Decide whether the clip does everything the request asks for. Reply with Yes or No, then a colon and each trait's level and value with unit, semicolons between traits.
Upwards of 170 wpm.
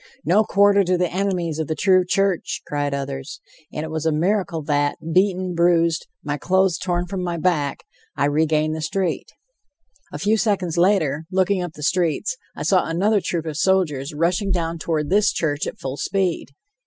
Yes: average, 180 wpm